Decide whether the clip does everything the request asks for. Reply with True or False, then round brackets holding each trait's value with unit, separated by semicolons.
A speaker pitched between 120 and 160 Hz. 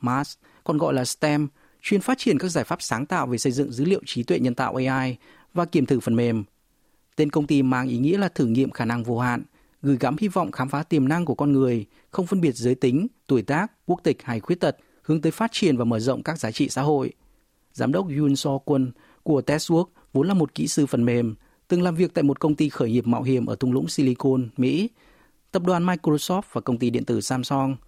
True (140 Hz)